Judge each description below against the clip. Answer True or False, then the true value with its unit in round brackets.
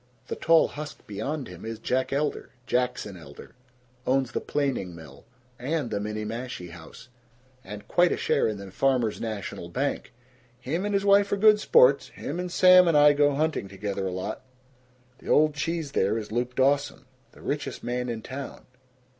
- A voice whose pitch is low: True (130 Hz)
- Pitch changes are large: True (6.2 semitones)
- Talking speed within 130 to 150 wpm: False (175 wpm)